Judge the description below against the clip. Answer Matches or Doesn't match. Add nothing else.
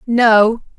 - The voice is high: Matches